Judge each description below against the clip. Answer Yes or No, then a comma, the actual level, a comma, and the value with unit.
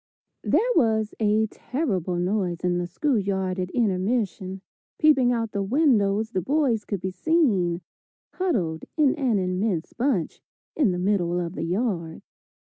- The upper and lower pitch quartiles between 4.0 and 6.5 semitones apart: Yes, average, 5.1 semitones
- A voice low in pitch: No, high, 200 Hz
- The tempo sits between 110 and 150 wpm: Yes, average, 145 wpm